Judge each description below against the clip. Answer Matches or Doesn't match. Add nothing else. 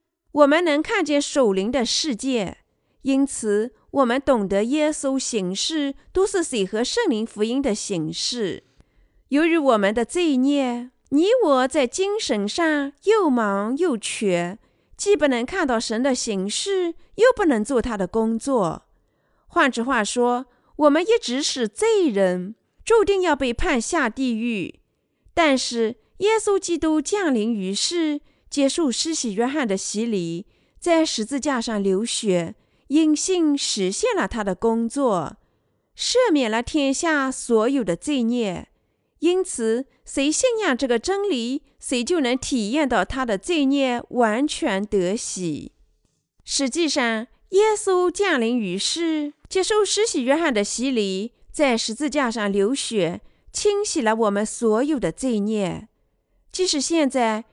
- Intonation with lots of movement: Matches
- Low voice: Doesn't match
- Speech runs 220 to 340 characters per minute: Doesn't match